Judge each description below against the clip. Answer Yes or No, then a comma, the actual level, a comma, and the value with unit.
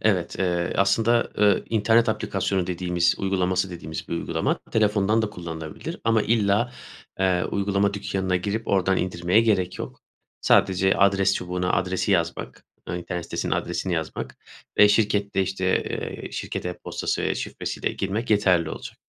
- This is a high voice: No, very low, 95 Hz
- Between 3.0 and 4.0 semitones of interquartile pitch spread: No, narrow, 2.5 semitones